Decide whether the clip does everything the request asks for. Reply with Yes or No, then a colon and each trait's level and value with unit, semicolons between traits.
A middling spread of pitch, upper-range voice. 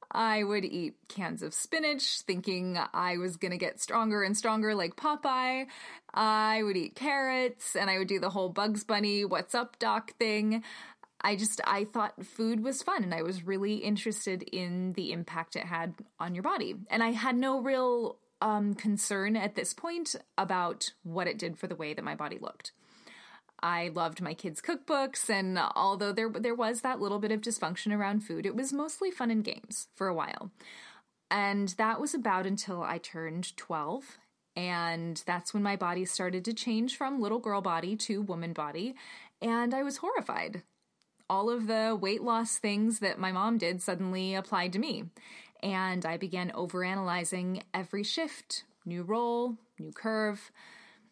Yes: average, 4.0 semitones; high, 205 Hz